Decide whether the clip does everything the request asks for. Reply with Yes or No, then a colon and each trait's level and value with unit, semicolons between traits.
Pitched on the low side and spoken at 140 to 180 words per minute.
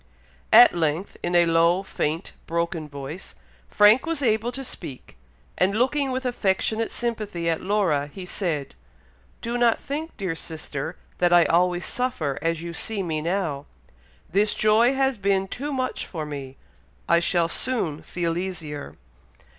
No: medium, 180 Hz; average, 150 wpm